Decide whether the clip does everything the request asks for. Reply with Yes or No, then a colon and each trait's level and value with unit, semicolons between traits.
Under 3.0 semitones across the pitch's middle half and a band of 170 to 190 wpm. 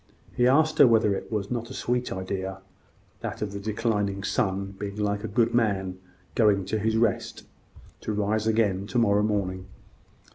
Yes: narrow, 2.5 semitones; average, 175 wpm